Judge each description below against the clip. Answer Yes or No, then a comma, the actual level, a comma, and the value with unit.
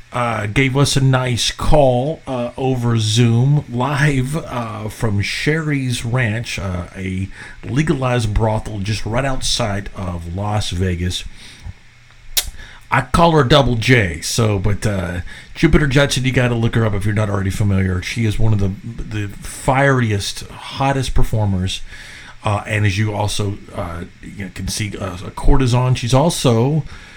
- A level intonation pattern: No, average, 4.4 semitones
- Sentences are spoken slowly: No, average, 145 wpm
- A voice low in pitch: Yes, low, 110 Hz